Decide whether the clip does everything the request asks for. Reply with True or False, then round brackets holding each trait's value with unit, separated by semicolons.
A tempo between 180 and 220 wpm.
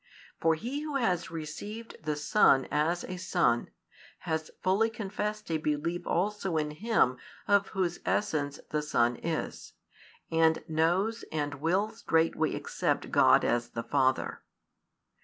False (135 wpm)